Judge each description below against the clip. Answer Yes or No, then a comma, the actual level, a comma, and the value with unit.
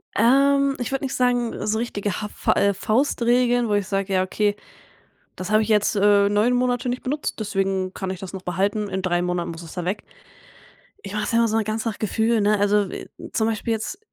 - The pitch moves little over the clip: No, average, 3.3 semitones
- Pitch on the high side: Yes, high, 210 Hz